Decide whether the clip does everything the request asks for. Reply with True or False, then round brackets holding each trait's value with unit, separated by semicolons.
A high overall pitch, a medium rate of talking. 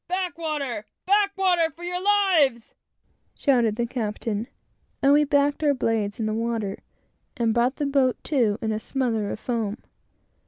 True (255 Hz; 160 wpm)